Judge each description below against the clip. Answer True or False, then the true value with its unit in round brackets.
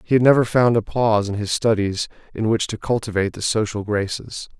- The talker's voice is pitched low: True (110 Hz)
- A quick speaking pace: True (210 wpm)